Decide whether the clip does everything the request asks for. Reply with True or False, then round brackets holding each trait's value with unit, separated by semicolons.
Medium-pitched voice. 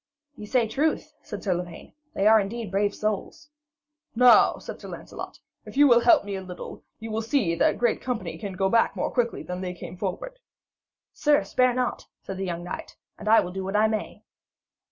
False (215 Hz)